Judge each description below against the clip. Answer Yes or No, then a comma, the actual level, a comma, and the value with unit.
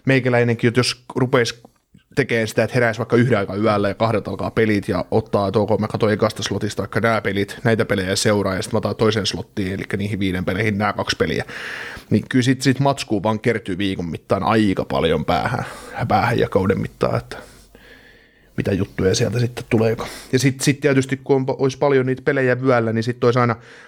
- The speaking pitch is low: Yes, low, 115 Hz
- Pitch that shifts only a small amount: No, average, 3.5 semitones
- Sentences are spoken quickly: Yes, fast, 200 wpm